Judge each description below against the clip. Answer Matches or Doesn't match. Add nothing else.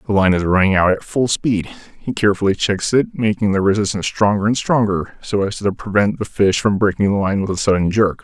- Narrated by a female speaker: Doesn't match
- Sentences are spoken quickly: Matches